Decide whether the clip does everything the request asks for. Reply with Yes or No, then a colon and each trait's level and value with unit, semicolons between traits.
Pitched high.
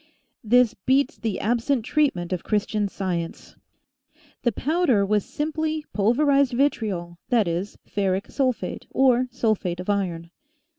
Yes: high, 220 Hz